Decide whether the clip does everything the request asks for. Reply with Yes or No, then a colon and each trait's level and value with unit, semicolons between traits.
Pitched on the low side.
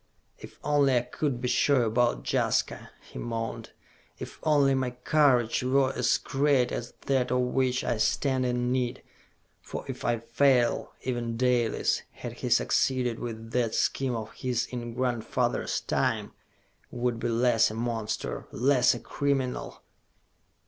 Yes: low, 125 Hz